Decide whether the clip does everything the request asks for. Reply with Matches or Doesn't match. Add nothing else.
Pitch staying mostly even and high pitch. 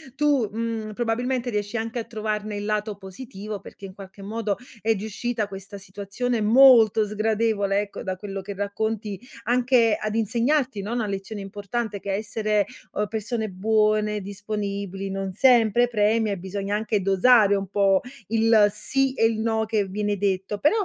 Matches